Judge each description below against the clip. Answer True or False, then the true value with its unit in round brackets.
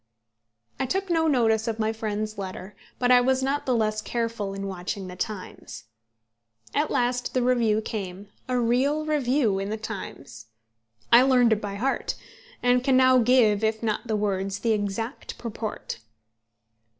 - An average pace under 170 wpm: True (160 wpm)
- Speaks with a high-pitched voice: True (225 Hz)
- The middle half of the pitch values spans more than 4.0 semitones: False (3.5 semitones)